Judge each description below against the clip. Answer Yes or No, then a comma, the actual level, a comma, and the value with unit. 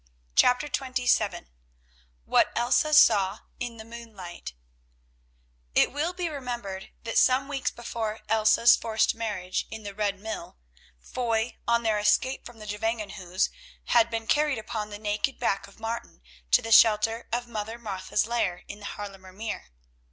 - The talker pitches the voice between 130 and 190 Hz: No, high, 225 Hz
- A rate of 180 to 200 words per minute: No, average, 150 wpm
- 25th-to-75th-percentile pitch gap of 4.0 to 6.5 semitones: No, narrow, 2.5 semitones